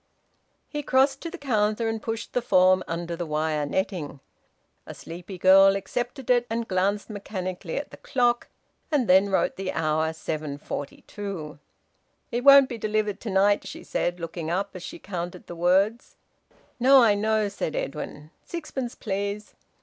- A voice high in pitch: Yes, high, 200 Hz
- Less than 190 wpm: Yes, average, 155 wpm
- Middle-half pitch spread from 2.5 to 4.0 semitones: No, average, 4.9 semitones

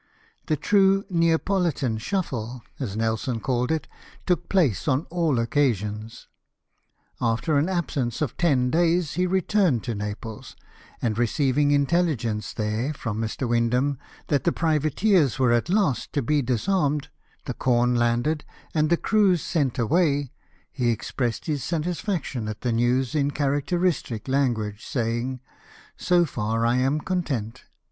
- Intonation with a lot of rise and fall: Yes, wide, 5.7 semitones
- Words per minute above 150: No, average, 140 wpm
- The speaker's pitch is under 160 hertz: Yes, low, 135 Hz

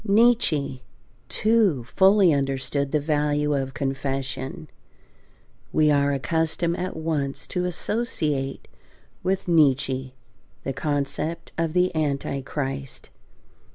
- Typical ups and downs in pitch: Yes, average, 3.9 semitones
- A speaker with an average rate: No, slow, 95 wpm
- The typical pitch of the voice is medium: Yes, medium, 150 Hz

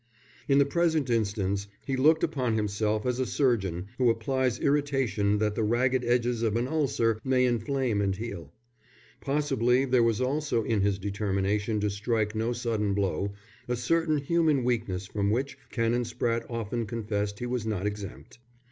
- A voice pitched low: Yes, low, 115 Hz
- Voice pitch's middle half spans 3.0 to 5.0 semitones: Yes, average, 3.8 semitones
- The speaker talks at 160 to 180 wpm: Yes, average, 165 wpm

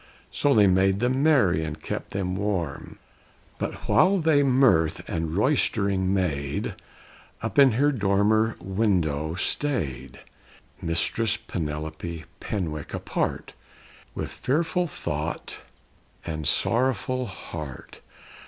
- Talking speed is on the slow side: Yes, slow, 105 wpm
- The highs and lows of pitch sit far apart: Yes, wide, 7.9 semitones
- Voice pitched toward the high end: No, very low, 95 Hz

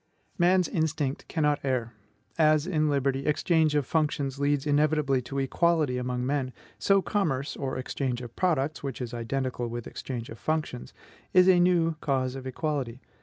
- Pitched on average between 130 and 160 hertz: Yes, medium, 140 Hz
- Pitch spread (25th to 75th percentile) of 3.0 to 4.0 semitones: Yes, average, 3.4 semitones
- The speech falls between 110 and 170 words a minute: Yes, average, 160 wpm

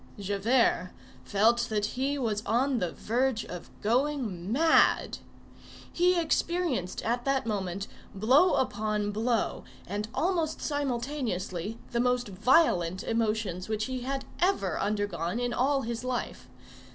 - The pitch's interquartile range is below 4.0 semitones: No, average, 4.6 semitones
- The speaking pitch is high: Yes, high, 230 Hz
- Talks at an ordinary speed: No, slow, 125 wpm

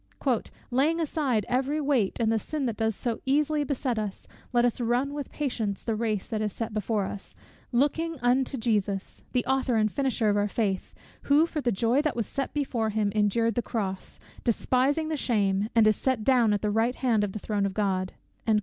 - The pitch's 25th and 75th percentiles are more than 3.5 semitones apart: Yes, average, 4.1 semitones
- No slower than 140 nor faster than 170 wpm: No, fast, 205 wpm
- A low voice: No, high, 230 Hz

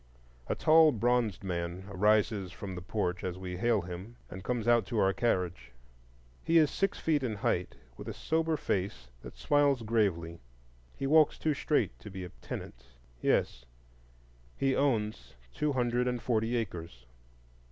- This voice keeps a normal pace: Yes, average, 155 wpm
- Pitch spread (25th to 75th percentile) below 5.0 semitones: No, wide, 5.6 semitones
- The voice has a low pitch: Yes, low, 105 Hz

